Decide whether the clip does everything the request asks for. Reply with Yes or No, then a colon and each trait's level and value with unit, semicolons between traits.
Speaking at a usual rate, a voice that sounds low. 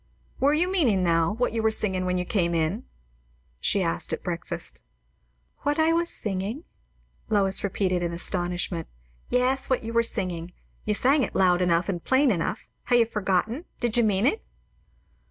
No: average, 170 wpm; high, 205 Hz